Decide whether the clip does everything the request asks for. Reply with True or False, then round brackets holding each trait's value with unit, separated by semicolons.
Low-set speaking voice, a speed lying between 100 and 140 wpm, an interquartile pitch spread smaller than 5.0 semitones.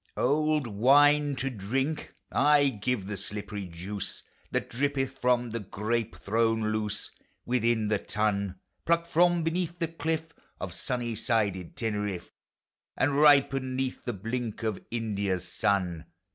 False (115 Hz; 135 wpm; 5.4 semitones)